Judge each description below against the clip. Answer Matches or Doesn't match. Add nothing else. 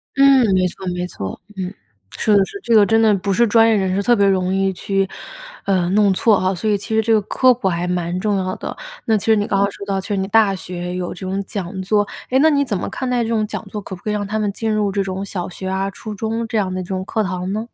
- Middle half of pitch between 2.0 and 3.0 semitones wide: Matches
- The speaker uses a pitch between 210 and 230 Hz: Doesn't match